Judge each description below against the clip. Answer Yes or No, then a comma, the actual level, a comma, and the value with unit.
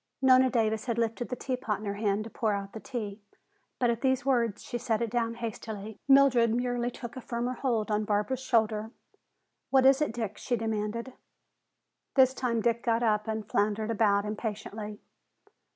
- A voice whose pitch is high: Yes, high, 230 Hz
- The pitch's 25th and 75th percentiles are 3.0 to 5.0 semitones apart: No, narrow, 2.5 semitones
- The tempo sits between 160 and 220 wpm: Yes, average, 180 wpm